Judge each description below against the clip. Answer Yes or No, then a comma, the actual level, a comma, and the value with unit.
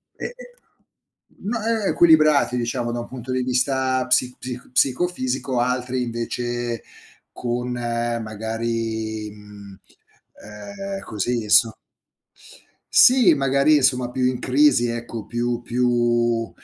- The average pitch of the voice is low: Yes, low, 120 Hz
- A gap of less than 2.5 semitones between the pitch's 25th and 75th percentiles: Yes, narrow, 1.7 semitones